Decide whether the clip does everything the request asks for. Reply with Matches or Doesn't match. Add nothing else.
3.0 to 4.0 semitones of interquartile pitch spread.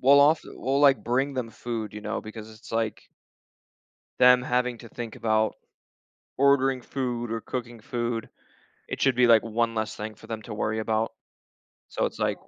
Doesn't match